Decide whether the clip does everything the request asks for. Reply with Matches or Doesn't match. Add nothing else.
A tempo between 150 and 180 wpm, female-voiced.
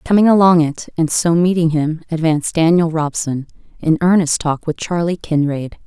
Matches